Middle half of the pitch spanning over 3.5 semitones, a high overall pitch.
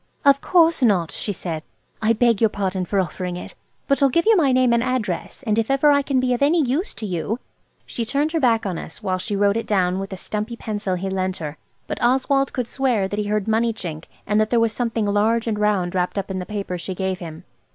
Yes: average, 4.8 semitones; high, 215 Hz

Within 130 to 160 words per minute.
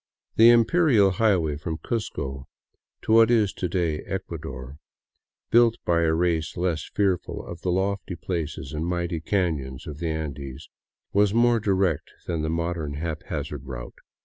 Yes: average, 145 wpm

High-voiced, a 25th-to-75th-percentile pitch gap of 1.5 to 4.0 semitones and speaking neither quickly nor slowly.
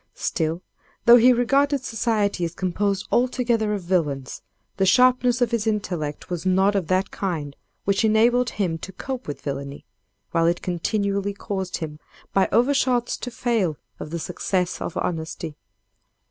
No: high, 195 Hz; wide, 5.6 semitones; average, 150 wpm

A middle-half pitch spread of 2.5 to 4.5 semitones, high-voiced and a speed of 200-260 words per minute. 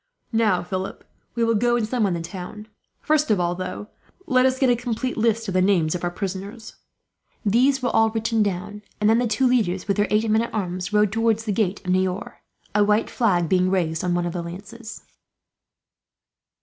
Yes: average, 3.8 semitones; high, 210 Hz; fast, 205 wpm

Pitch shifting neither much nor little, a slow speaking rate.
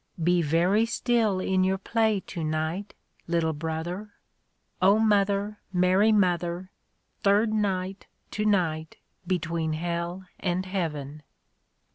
Yes: average, 3.3 semitones; slow, 115 wpm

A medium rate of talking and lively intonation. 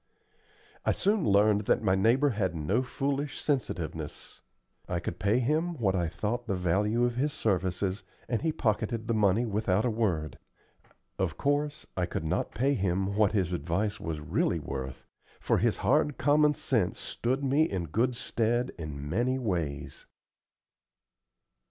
Yes: average, 155 wpm; wide, 5.7 semitones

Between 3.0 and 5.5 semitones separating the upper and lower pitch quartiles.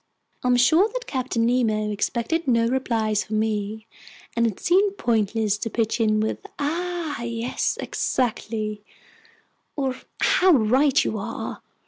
Yes: average, 4.2 semitones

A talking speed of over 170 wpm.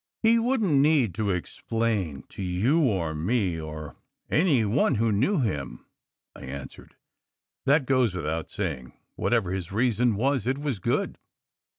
No: average, 150 wpm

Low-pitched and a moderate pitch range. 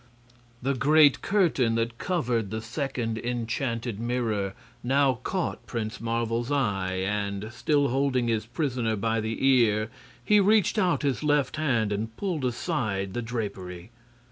Yes: low, 120 Hz; average, 3.9 semitones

